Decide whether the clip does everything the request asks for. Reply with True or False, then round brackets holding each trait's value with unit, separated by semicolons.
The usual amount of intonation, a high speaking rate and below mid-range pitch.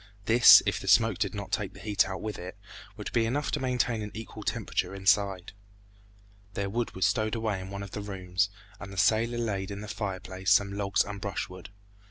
False (2.2 semitones; 210 wpm; 100 Hz)